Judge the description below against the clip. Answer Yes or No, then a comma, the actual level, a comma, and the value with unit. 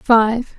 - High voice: Yes, high, 230 Hz